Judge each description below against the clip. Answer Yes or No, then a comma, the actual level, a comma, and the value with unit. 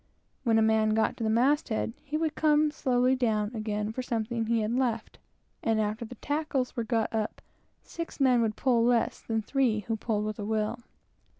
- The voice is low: No, high, 230 Hz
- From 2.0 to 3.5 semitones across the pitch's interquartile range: Yes, average, 2.8 semitones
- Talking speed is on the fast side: Yes, fast, 210 wpm